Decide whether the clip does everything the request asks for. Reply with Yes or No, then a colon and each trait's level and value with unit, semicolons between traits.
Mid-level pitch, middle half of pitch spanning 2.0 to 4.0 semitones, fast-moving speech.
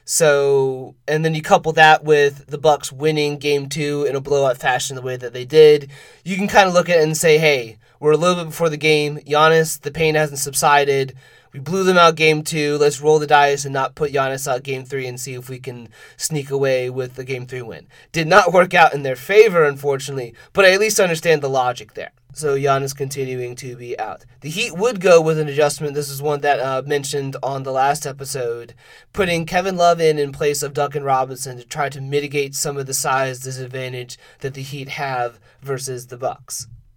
Yes: medium, 145 Hz; average, 2.7 semitones; fast, 225 wpm